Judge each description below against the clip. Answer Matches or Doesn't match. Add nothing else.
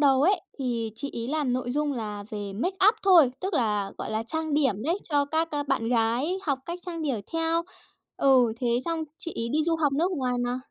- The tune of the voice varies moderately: Doesn't match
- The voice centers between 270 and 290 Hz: Matches